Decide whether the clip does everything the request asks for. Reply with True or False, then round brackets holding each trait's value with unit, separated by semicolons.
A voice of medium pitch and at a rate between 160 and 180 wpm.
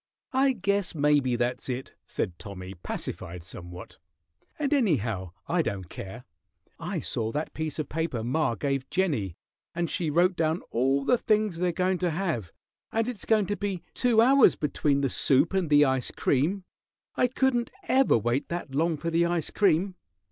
True (160 Hz; 170 wpm)